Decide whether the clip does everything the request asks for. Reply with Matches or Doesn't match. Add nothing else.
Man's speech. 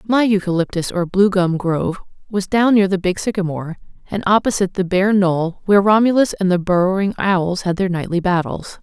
Doesn't match